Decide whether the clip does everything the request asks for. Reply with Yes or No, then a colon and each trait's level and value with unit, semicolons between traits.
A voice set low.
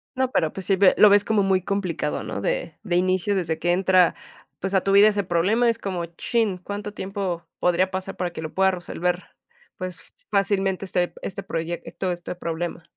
No: medium, 185 Hz